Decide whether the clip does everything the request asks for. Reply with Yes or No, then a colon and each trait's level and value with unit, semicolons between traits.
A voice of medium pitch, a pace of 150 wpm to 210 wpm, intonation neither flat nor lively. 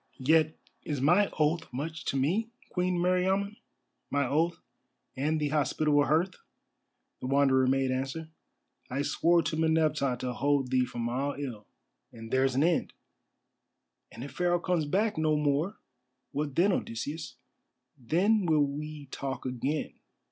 No: medium, 150 Hz; average, 140 wpm; average, 3.6 semitones